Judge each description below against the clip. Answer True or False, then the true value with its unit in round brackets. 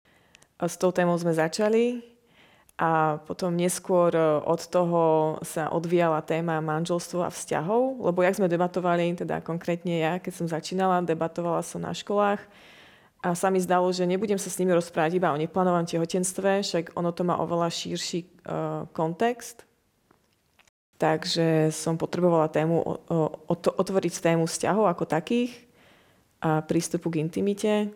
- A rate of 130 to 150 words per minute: True (140 wpm)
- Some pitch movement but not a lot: False (2.1 semitones)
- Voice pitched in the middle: True (175 Hz)